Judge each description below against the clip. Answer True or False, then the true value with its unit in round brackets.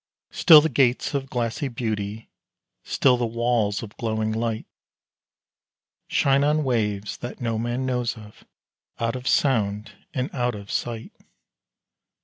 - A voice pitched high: False (120 Hz)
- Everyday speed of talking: False (130 wpm)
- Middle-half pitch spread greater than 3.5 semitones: False (2.8 semitones)